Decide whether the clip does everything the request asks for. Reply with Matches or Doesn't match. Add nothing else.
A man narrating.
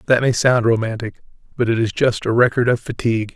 Matches